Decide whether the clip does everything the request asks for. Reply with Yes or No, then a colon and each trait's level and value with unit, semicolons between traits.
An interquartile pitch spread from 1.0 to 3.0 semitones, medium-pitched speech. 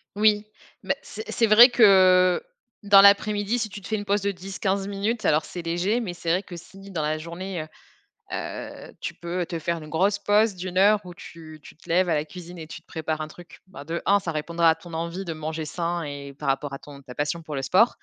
No: average, 3.8 semitones; medium, 175 Hz